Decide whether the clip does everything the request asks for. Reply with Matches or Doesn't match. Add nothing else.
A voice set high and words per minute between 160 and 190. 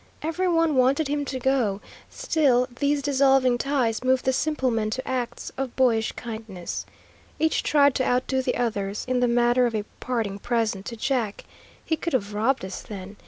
Matches